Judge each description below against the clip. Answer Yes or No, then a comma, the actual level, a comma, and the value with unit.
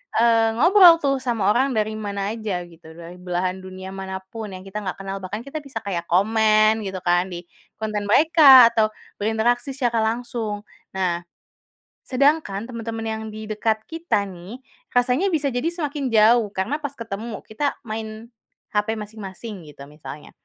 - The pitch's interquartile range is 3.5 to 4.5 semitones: Yes, average, 4.0 semitones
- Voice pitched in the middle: No, high, 220 Hz